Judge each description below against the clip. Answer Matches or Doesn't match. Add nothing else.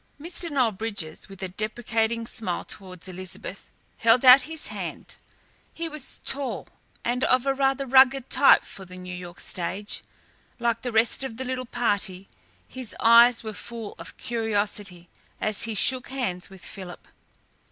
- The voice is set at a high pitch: Matches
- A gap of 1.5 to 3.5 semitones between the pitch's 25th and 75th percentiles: Doesn't match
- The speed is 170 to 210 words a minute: Doesn't match